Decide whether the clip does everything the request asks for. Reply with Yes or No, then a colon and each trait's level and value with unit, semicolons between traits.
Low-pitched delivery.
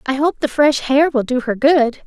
No: very high, 275 Hz